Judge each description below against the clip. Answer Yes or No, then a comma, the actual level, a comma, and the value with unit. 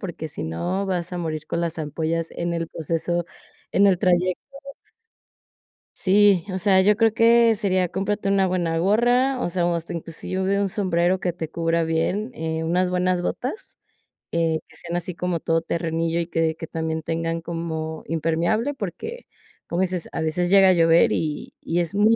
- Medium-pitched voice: Yes, medium, 175 Hz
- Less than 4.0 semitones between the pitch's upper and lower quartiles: Yes, average, 2.9 semitones